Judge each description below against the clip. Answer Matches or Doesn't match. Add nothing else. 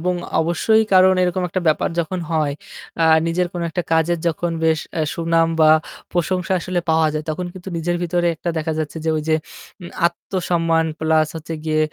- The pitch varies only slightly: Matches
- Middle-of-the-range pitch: Matches